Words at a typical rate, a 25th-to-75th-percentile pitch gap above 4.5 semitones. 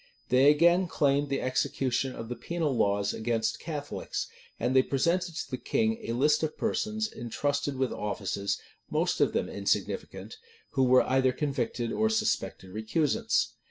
Yes: average, 155 wpm; wide, 5.4 semitones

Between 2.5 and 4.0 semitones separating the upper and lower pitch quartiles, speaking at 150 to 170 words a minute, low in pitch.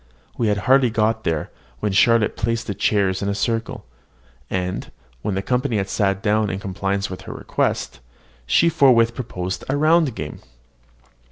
Yes: average, 3.2 semitones; average, 165 wpm; low, 105 Hz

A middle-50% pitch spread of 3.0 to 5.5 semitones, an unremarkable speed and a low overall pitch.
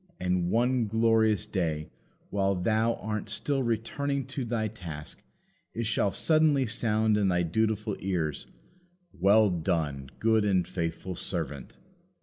No: average, 4.0 semitones; slow, 130 wpm; low, 105 Hz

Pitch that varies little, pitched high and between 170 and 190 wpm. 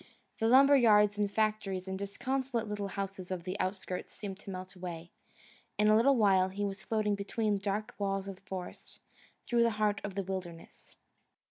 Yes: narrow, 2.1 semitones; high, 200 Hz; average, 175 wpm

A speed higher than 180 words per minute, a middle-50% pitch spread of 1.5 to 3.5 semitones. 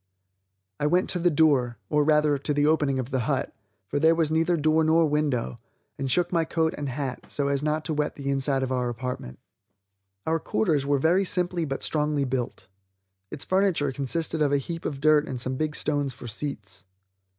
Yes: average, 200 wpm; average, 3.0 semitones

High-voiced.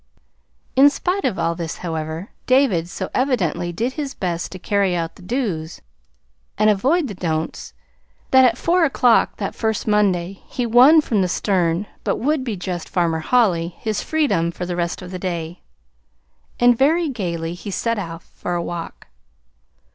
Yes: high, 195 Hz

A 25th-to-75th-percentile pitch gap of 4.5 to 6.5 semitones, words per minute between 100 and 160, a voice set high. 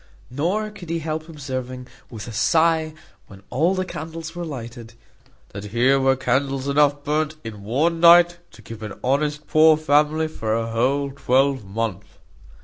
No: average, 4.8 semitones; average, 155 wpm; medium, 140 Hz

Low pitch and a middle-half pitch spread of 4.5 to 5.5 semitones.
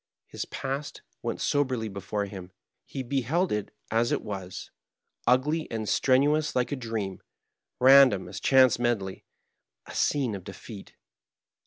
Yes: low, 120 Hz; average, 5.1 semitones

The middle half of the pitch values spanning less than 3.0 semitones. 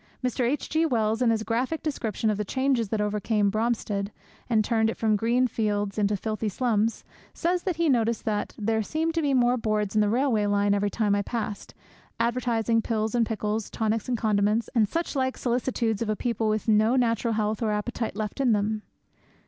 Yes: narrow, 2.4 semitones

